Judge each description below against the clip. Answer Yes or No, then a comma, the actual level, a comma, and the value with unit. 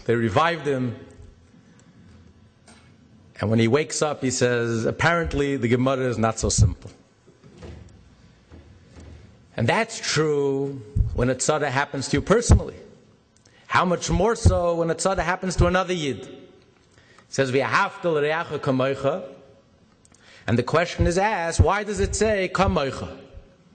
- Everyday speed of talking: No, slow, 130 wpm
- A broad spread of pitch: Yes, wide, 6.0 semitones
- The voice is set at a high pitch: No, low, 135 Hz